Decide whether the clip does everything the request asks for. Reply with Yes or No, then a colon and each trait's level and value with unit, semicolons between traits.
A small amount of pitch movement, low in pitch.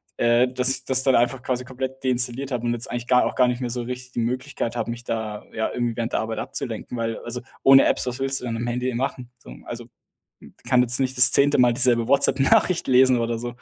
Yes: narrow, 1.6 semitones; low, 125 Hz